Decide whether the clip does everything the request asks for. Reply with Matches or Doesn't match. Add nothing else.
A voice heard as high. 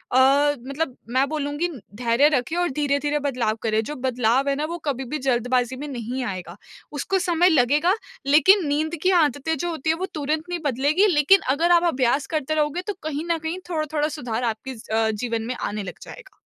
Matches